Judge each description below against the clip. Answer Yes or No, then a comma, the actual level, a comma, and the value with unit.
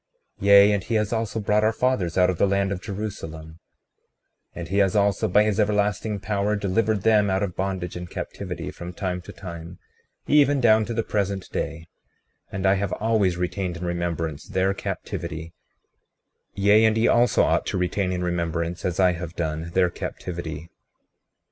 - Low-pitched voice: Yes, very low, 95 Hz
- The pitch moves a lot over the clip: No, average, 3.0 semitones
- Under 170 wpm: No, average, 180 wpm